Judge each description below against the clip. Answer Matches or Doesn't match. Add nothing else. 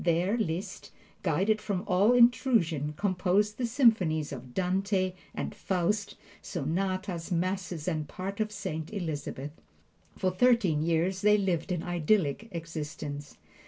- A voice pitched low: Doesn't match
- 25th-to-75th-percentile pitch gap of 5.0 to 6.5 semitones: Doesn't match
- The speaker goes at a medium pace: Doesn't match